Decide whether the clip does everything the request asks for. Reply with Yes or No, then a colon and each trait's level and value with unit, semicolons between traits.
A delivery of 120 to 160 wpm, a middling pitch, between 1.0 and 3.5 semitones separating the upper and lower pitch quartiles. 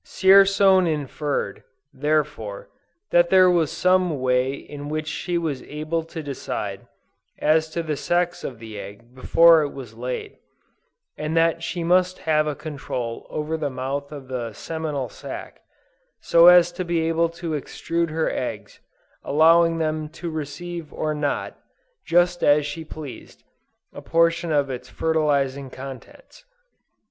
Yes: average, 145 wpm; medium, 155 Hz; average, 3.2 semitones